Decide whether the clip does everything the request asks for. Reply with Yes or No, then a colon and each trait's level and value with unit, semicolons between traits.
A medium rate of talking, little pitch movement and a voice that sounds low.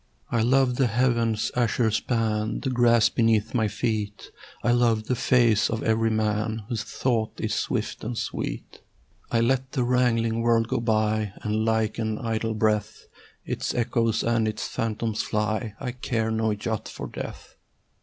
Yes: average, 160 wpm; narrow, 1.6 semitones; low, 115 Hz